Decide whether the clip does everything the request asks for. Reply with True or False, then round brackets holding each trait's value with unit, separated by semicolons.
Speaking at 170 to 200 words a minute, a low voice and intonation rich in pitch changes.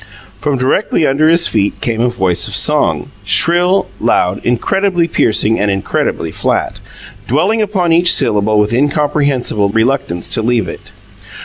False (140 wpm; 130 Hz; 8.0 semitones)